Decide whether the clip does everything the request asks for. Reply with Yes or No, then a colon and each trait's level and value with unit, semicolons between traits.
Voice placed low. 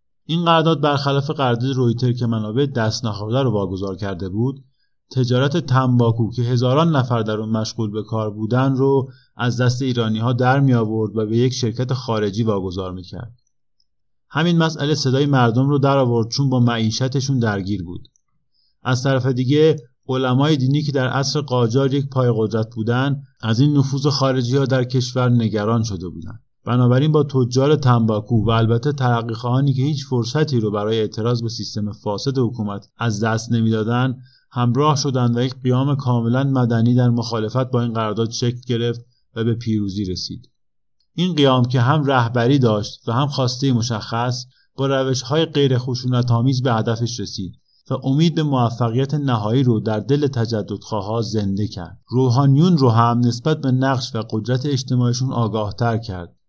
Yes: low, 125 Hz